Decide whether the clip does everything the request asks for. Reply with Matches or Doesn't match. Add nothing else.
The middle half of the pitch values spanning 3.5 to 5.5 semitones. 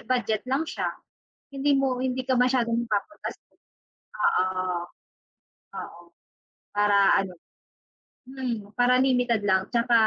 Matches